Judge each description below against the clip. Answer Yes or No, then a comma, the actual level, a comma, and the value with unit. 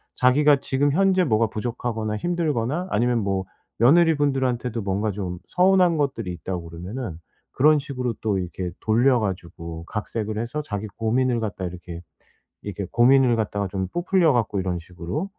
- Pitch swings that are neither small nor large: No, wide, 6.2 semitones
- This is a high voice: No, low, 115 Hz